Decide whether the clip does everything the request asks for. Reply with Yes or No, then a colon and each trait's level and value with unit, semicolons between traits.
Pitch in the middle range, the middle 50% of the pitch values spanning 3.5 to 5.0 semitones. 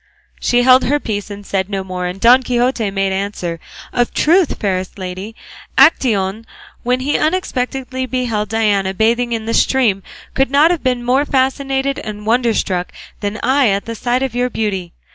No: high, 230 Hz; average, 4.5 semitones